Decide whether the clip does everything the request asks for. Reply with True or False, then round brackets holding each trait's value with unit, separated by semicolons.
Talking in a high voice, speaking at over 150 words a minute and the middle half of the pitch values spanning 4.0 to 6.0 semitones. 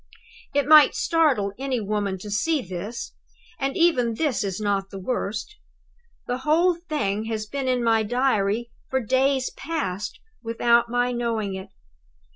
False (235 Hz; 145 wpm; 4.7 semitones)